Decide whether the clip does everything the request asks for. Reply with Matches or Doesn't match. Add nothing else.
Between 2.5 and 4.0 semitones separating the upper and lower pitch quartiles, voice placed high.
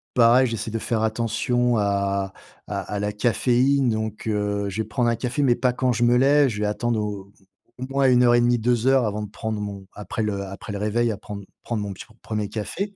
Doesn't match